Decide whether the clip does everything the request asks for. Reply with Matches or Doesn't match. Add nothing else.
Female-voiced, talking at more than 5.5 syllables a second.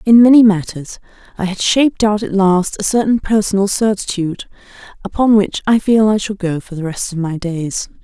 Doesn't match